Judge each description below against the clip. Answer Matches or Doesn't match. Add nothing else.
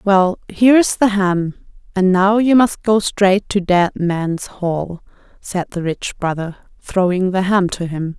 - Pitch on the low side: Doesn't match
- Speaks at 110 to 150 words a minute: Doesn't match